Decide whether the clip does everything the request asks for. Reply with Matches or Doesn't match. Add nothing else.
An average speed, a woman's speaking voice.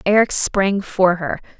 Matches